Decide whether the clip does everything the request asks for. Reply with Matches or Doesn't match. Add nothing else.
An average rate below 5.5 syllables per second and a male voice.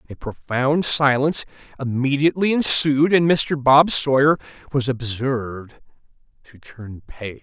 Matches